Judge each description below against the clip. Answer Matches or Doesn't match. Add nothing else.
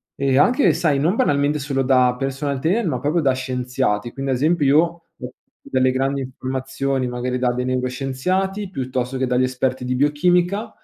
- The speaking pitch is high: Doesn't match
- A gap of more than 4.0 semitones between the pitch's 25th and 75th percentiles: Doesn't match